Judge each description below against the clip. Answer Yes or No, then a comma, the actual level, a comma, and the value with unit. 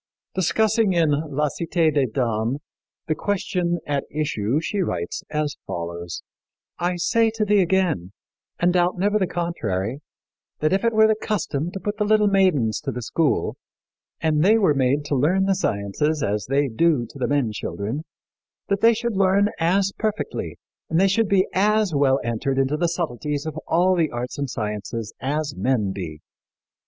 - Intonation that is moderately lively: No, wide, 6.7 semitones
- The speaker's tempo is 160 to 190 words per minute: Yes, average, 175 wpm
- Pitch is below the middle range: No, medium, 155 Hz